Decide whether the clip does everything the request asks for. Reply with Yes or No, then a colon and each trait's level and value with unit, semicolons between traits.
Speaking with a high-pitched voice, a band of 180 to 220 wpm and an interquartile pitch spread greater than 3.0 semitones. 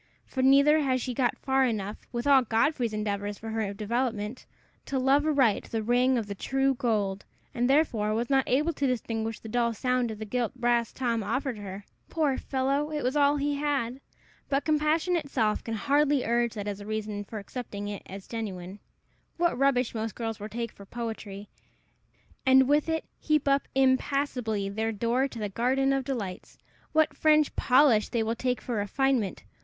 Yes: high, 245 Hz; average, 185 wpm; average, 4.0 semitones